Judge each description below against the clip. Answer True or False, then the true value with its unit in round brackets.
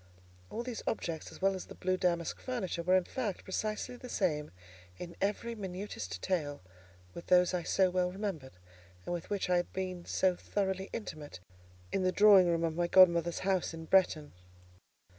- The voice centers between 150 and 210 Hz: True (185 Hz)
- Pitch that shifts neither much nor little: False (2.3 semitones)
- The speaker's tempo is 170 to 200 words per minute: True (180 wpm)